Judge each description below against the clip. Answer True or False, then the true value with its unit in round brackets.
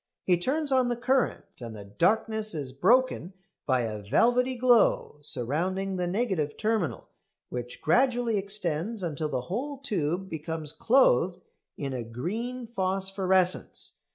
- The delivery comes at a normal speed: False (130 wpm)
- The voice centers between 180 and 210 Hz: True (190 Hz)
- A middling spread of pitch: False (7.7 semitones)